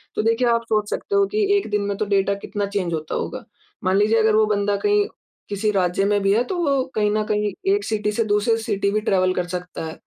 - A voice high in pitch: Yes, high, 210 Hz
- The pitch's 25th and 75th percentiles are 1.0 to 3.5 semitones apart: Yes, narrow, 2.4 semitones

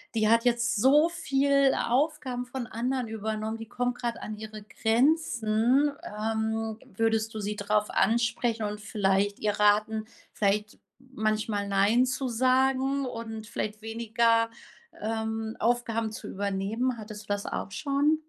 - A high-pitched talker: Yes, high, 225 Hz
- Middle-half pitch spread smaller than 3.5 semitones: Yes, average, 2.7 semitones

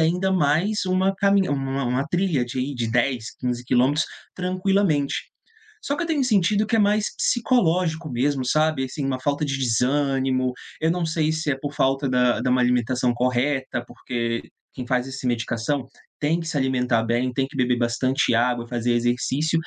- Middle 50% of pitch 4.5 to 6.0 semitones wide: Yes, average, 4.8 semitones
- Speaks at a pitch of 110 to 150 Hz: Yes, low, 135 Hz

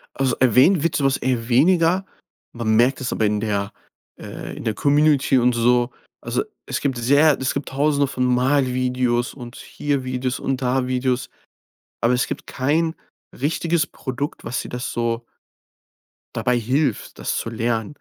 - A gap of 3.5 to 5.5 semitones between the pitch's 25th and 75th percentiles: No, average, 2.8 semitones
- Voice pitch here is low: Yes, low, 130 Hz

